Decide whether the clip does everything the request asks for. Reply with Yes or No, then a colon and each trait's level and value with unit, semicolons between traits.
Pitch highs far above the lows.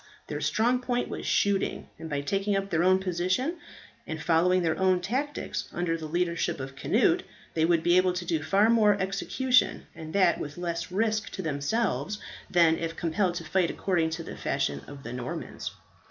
No: average, 3.5 semitones